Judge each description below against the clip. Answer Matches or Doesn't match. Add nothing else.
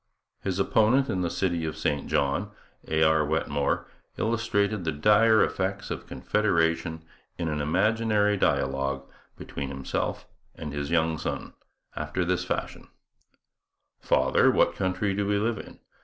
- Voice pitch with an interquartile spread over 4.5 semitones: Matches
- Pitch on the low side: Matches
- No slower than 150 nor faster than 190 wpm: Doesn't match